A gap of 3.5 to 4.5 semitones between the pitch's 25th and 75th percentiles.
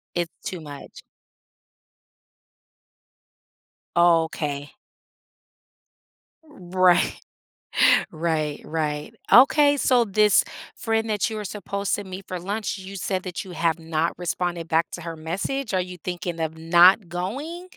Yes: average, 3.8 semitones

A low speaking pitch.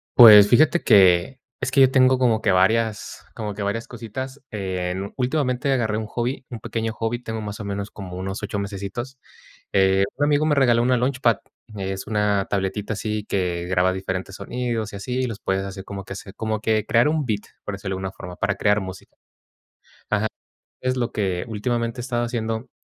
Yes: low, 110 Hz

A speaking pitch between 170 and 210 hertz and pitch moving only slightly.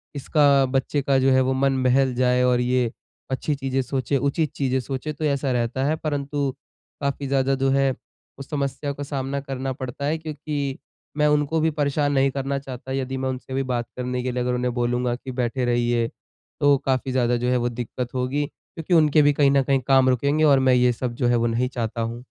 No: low, 135 Hz; narrow, 2.0 semitones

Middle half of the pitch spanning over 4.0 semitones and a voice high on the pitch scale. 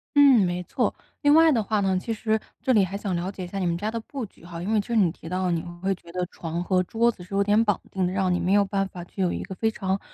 No: average, 3.3 semitones; high, 195 Hz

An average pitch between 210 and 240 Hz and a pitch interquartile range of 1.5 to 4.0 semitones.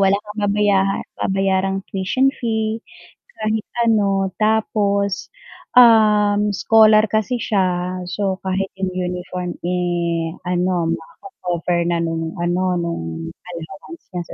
No: high, 195 Hz; average, 2.9 semitones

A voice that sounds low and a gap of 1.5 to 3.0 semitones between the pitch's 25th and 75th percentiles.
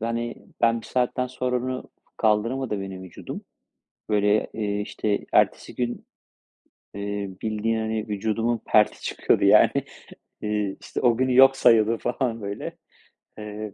Yes: low, 110 Hz; narrow, 2.4 semitones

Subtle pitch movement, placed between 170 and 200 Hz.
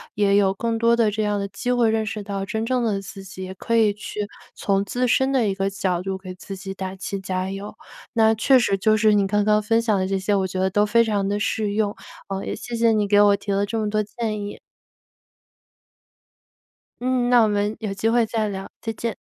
No: narrow, 2.3 semitones; high, 210 Hz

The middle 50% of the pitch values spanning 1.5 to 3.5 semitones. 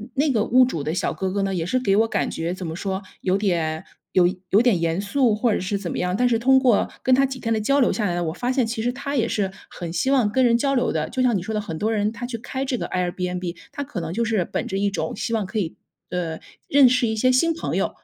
No: wide, 5.5 semitones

